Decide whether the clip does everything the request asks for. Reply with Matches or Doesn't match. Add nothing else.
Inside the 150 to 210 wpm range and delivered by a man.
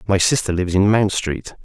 Doesn't match